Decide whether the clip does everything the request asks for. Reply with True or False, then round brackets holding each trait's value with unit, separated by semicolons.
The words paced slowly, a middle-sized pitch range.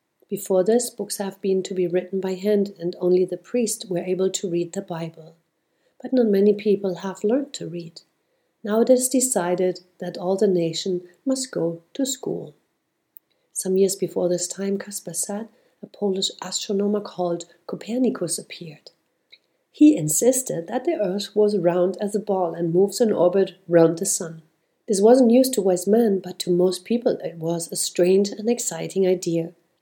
False (175 wpm; 3.1 semitones)